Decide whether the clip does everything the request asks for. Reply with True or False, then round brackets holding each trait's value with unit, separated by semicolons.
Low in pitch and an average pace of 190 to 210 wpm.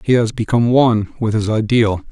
True (115 Hz; 200 wpm)